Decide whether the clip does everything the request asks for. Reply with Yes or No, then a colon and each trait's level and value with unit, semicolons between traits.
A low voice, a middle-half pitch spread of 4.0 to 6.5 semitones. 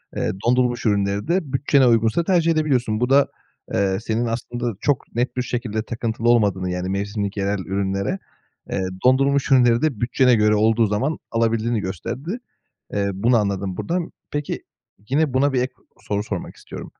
Yes: low, 115 Hz; average, 4.4 semitones